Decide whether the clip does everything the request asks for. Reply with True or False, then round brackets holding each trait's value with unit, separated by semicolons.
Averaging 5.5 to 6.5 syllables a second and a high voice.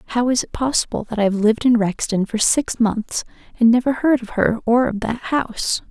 False (5.2 syllables/s; 230 Hz)